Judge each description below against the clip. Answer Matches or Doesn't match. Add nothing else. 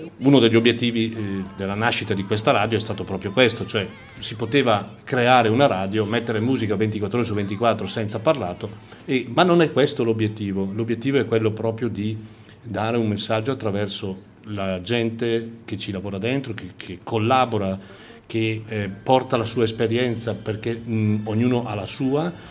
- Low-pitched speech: Matches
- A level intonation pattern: Matches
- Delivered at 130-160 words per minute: Matches